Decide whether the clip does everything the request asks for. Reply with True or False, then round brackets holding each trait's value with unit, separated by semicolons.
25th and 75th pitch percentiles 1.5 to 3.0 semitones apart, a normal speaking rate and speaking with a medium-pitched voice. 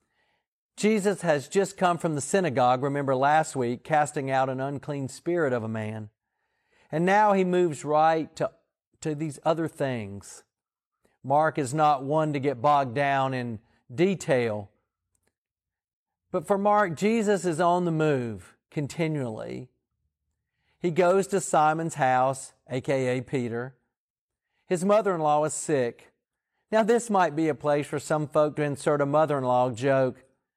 False (4.8 semitones; 150 wpm; 150 Hz)